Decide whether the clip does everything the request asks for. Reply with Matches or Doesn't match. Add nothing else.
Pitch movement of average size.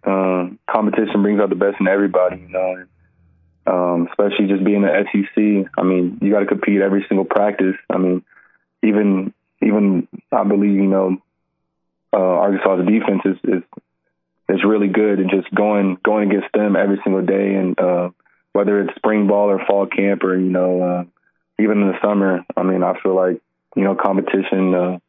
Doesn't match